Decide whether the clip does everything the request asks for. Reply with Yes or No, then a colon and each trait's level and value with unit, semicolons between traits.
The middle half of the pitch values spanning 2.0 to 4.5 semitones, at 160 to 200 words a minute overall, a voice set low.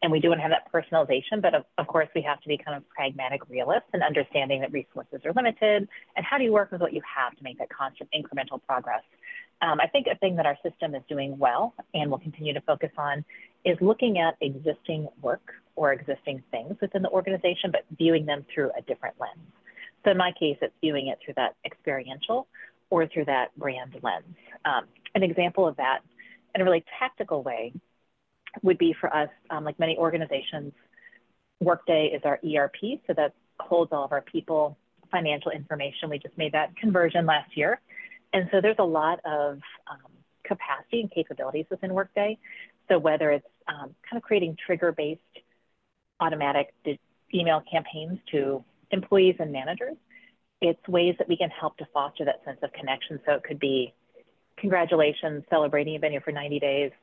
No: average, 4.2 semitones; average, 190 wpm; medium, 160 Hz